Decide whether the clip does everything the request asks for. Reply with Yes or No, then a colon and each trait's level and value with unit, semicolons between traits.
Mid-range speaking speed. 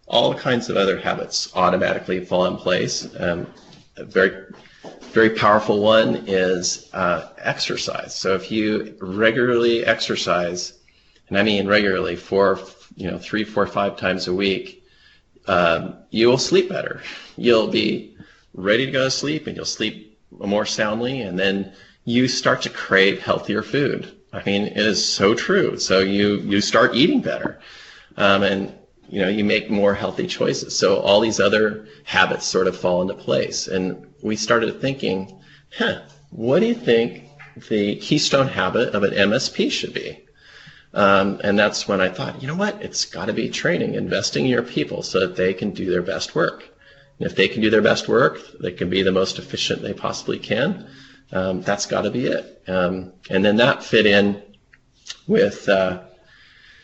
Yes: average, 175 wpm